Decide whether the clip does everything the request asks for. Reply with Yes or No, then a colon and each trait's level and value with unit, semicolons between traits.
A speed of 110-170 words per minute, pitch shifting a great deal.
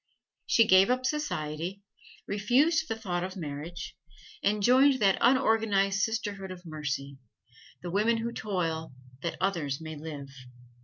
Yes: slow, 135 wpm; wide, 5.7 semitones